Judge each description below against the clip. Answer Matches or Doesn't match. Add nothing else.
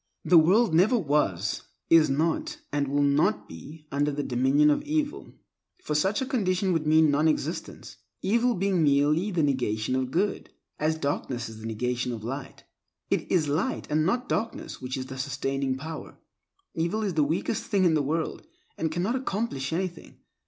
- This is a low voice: Doesn't match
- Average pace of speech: Matches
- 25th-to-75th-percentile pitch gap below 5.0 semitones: Doesn't match